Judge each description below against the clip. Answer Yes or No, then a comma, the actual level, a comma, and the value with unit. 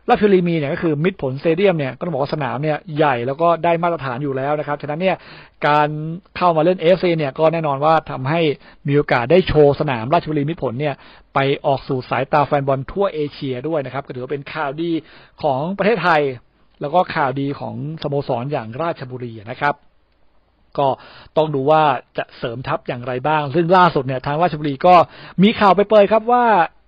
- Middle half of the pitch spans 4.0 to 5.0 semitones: No, average, 3.5 semitones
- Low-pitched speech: No, medium, 150 Hz